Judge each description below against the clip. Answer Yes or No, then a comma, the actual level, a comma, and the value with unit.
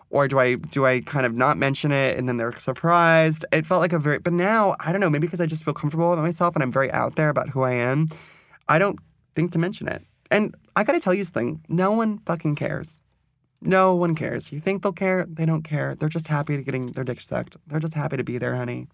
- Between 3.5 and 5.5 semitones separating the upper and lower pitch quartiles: Yes, average, 4.3 semitones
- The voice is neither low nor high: Yes, medium, 155 Hz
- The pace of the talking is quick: Yes, fast, 265 wpm